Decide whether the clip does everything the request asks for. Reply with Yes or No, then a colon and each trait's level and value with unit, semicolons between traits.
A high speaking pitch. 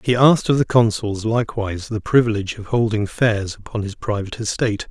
No: low, 110 Hz